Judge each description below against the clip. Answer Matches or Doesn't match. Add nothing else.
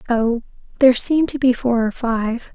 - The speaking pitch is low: Doesn't match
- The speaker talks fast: Doesn't match